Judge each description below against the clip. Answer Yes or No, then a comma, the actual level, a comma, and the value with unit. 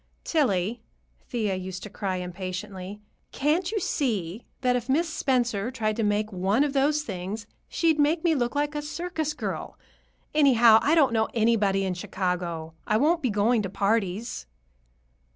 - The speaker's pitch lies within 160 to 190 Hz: No, high, 225 Hz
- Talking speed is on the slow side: No, average, 160 wpm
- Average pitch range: No, wide, 6.9 semitones